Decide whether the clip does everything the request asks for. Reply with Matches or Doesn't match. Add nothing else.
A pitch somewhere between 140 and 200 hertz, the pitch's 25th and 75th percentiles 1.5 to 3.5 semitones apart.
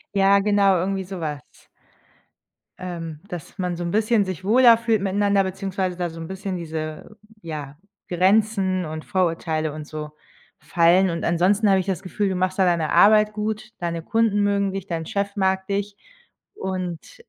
Matches